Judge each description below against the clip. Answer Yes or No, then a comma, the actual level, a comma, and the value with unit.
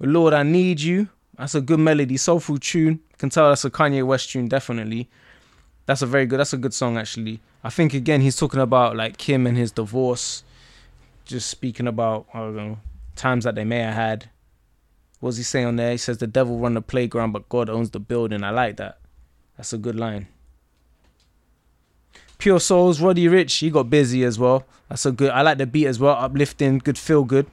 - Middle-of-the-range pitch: No, low, 125 Hz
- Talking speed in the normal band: No, fast, 210 wpm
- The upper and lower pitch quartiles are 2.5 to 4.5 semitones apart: Yes, average, 3.8 semitones